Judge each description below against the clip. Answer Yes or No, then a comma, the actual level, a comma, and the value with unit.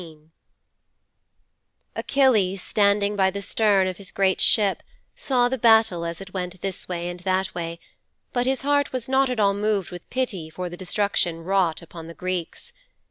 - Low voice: No, high, 195 Hz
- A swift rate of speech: No, average, 175 wpm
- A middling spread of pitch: Yes, average, 3.7 semitones